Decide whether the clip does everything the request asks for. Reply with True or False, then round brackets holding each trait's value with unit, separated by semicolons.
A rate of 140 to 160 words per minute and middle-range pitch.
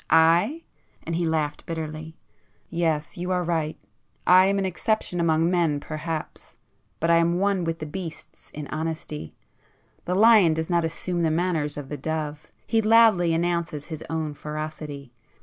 True (145 wpm; 165 Hz)